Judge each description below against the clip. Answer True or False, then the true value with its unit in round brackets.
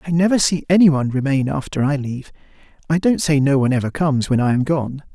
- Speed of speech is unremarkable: False (235 wpm)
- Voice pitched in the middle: True (145 Hz)